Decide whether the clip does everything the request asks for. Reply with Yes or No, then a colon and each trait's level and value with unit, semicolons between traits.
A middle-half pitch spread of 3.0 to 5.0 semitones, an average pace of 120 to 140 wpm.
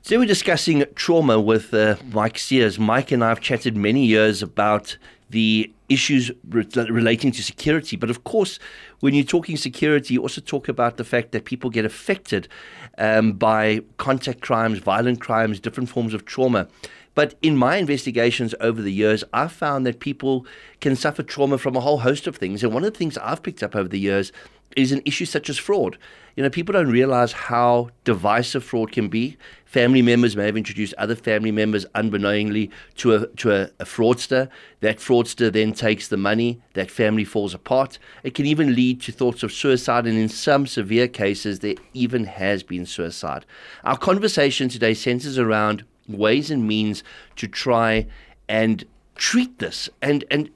No: average, 3.7 semitones; average, 185 wpm